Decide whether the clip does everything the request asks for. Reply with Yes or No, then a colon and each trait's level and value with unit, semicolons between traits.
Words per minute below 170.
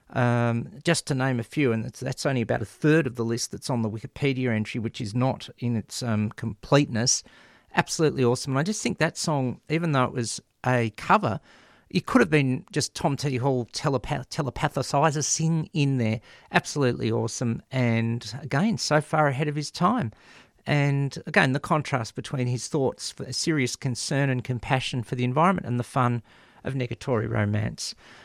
No: average, 185 wpm